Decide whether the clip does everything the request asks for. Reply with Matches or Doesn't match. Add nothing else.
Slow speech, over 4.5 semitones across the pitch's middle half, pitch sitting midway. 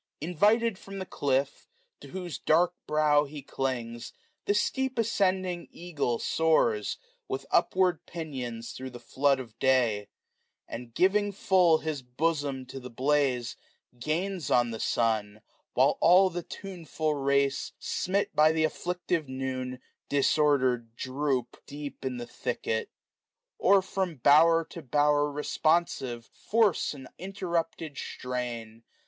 Matches